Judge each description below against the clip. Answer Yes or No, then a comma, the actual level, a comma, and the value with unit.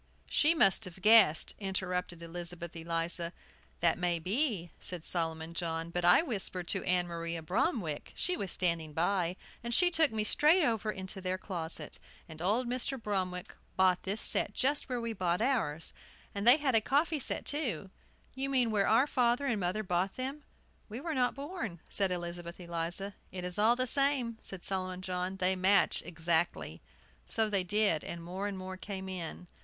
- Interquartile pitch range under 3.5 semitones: No, average, 5.2 semitones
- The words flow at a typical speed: Yes, average, 180 wpm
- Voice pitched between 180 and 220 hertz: Yes, high, 190 Hz